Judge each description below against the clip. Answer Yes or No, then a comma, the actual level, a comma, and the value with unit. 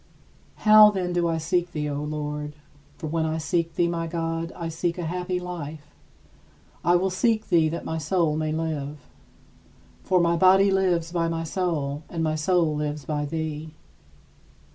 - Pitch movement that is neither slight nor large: No, narrow, 2.3 semitones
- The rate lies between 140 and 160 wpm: No, average, 170 wpm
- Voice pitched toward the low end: No, medium, 165 Hz